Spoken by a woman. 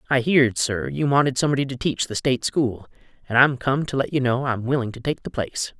No: male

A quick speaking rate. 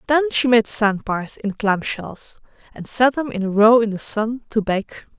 Yes: fast, 220 wpm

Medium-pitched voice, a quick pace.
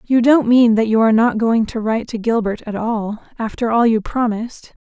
No: high, 225 Hz; fast, 210 wpm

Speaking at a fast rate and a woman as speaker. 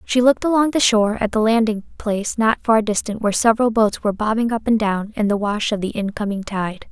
Yes: fast, 235 wpm; female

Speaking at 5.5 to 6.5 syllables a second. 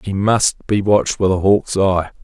No: 4.8 syllables/s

